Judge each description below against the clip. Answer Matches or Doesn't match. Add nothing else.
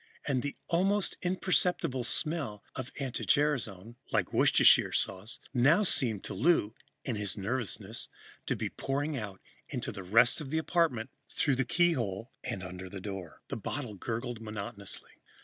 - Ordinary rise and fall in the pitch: Doesn't match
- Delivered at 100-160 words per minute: Matches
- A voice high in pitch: Doesn't match